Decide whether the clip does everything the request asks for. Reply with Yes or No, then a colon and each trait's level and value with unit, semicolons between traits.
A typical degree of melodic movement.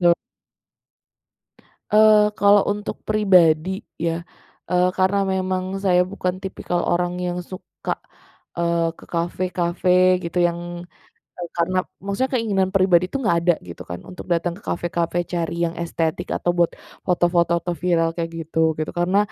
No: narrow, 1.8 semitones